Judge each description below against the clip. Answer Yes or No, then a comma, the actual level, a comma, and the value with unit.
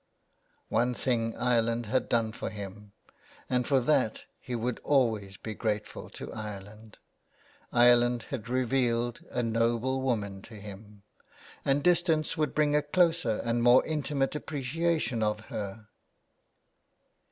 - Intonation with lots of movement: No, average, 3.6 semitones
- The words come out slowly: Yes, slow, 130 wpm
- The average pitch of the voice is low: Yes, low, 120 Hz